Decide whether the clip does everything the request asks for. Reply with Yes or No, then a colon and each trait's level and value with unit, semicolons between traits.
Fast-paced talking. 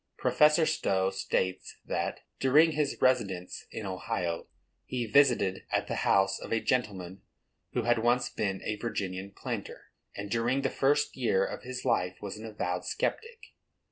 No: average, 155 wpm